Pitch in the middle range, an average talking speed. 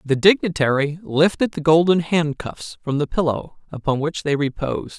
Yes: medium, 155 Hz; average, 155 wpm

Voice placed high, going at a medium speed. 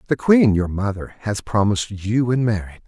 No: low, 110 Hz; average, 190 wpm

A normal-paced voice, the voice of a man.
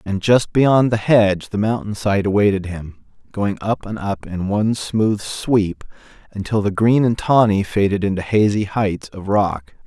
Yes: average, 170 wpm; male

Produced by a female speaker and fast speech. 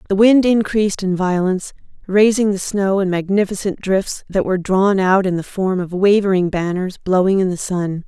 No: female; average, 185 wpm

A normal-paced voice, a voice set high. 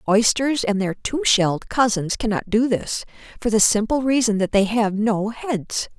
Yes: average, 180 wpm; high, 220 Hz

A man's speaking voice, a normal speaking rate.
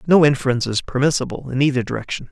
Yes: male; average, 180 wpm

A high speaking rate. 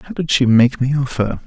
Yes: fast, 245 wpm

